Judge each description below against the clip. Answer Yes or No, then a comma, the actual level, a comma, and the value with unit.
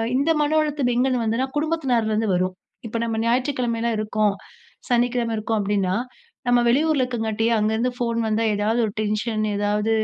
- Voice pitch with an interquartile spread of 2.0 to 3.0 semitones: Yes, narrow, 2.6 semitones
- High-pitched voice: Yes, high, 230 Hz